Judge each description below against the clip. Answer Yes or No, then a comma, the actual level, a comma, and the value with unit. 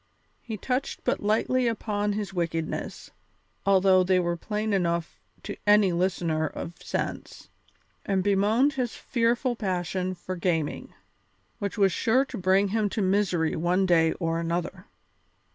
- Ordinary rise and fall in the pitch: Yes, average, 3.5 semitones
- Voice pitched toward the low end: No, high, 190 Hz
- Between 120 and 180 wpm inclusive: Yes, average, 140 wpm